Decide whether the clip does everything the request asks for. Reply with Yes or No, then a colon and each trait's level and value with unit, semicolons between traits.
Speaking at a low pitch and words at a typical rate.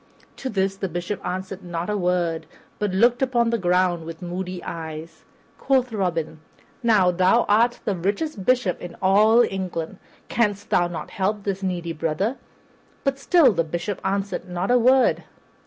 No: high, 190 Hz; average, 160 wpm